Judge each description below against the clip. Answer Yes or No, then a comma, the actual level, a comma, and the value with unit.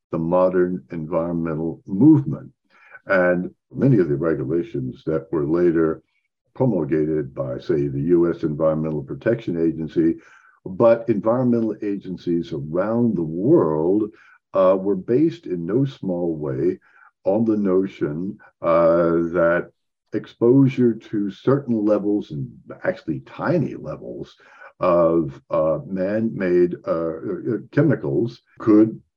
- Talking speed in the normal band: No, slow, 110 wpm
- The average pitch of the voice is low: Yes, very low, 90 Hz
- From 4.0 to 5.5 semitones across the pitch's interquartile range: Yes, average, 5.0 semitones